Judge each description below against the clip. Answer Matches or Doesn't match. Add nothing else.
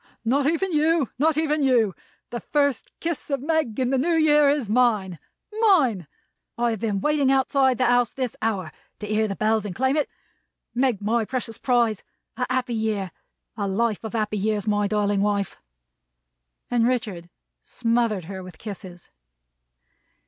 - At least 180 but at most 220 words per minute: Doesn't match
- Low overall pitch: Doesn't match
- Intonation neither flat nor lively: Matches